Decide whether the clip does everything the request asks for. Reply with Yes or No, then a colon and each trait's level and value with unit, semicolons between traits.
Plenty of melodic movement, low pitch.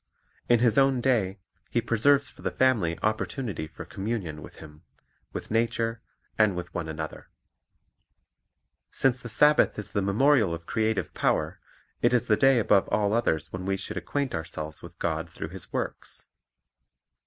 Yes: wide, 6.0 semitones; low, 105 Hz